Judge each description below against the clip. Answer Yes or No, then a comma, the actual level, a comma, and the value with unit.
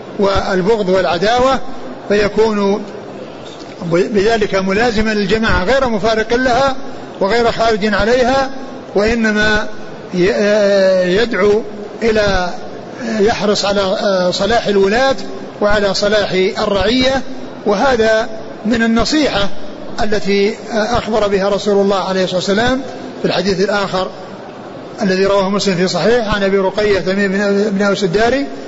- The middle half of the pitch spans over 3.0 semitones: No, narrow, 2.4 semitones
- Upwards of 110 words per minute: No, average, 100 wpm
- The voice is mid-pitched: No, high, 210 Hz